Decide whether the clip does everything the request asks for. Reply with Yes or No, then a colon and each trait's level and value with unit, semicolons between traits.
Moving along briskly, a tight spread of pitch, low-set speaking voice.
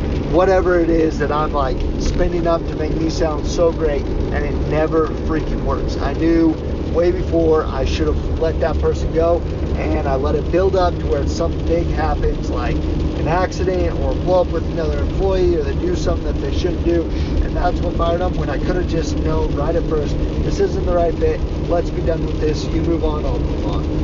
Yes: fast, 220 wpm; narrow, 1.5 semitones; very low, 75 Hz